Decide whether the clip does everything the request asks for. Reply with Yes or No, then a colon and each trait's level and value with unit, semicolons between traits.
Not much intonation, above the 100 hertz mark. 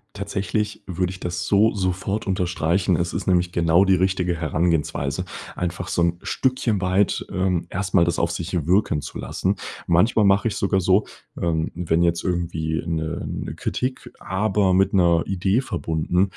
No: narrow, 2.2 semitones; very low, 90 Hz